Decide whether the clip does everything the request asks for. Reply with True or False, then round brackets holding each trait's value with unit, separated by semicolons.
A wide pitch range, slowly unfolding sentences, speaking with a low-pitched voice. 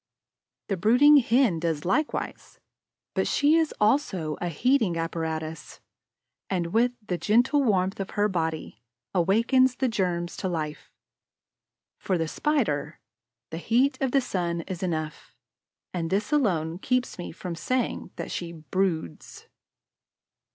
False (6.9 semitones; 130 wpm; 185 Hz)